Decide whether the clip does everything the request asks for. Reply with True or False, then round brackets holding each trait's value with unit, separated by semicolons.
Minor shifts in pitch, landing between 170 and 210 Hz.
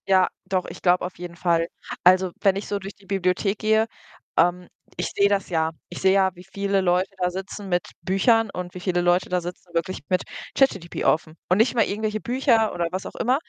True (2.2 semitones; 185 Hz)